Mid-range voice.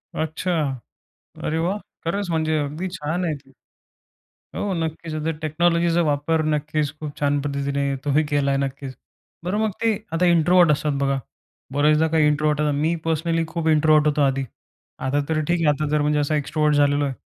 Yes: medium, 155 Hz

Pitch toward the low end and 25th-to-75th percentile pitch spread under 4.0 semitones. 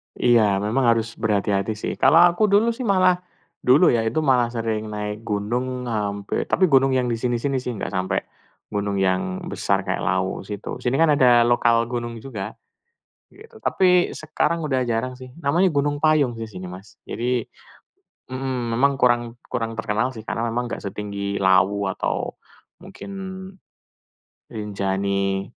No: low, 115 Hz; average, 4.6 semitones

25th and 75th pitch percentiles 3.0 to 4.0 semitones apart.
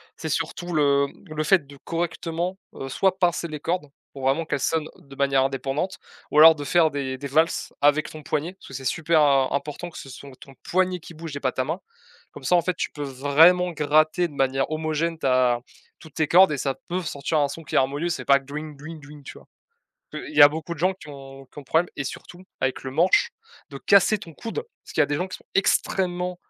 Yes: average, 3.7 semitones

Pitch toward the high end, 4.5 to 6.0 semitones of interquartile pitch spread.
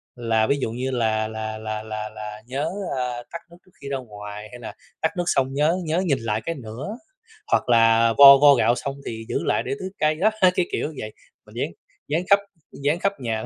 No: low, 125 Hz; wide, 5.5 semitones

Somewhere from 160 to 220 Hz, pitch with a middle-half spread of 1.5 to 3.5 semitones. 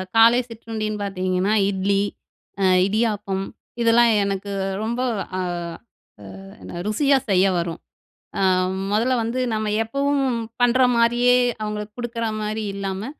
Yes: high, 215 Hz; average, 3.2 semitones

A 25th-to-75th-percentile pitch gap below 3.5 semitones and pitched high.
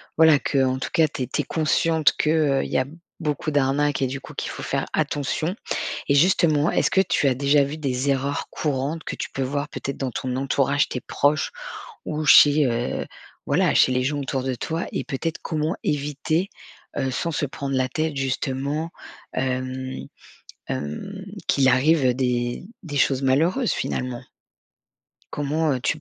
No: average, 2.9 semitones; medium, 140 Hz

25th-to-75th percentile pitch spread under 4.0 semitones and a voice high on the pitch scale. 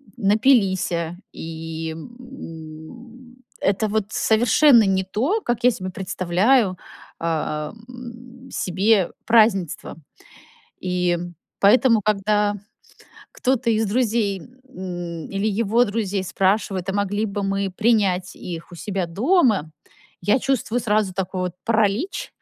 No: average, 4.3 semitones; high, 205 Hz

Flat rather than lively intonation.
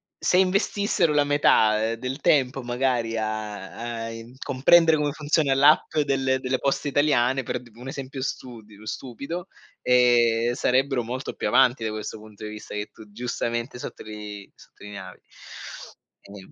No: average, 3.7 semitones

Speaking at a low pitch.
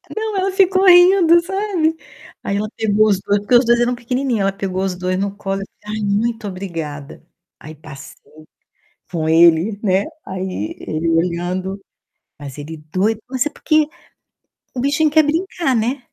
No: high, 205 Hz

